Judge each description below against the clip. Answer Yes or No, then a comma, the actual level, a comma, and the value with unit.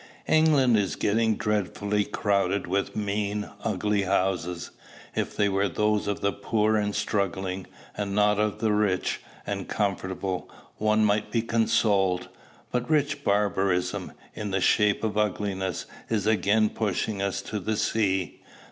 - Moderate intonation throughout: No, narrow, 1.7 semitones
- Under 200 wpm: Yes, average, 140 wpm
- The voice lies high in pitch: No, low, 105 Hz